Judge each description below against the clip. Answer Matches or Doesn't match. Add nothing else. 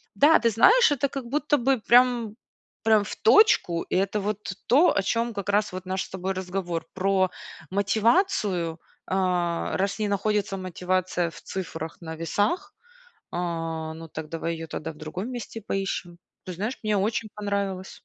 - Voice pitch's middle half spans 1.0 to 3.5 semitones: Doesn't match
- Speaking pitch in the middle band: Doesn't match